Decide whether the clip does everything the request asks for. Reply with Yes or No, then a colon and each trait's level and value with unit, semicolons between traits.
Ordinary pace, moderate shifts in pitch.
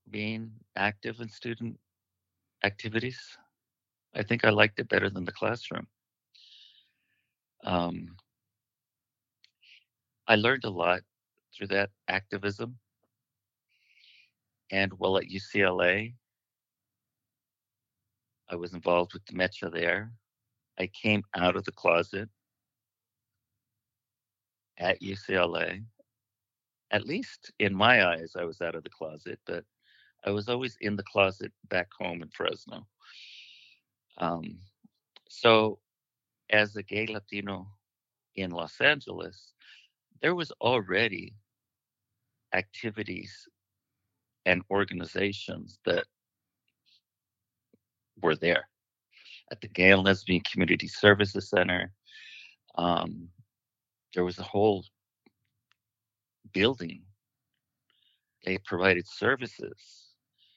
No: slow, 95 wpm; average, 3.2 semitones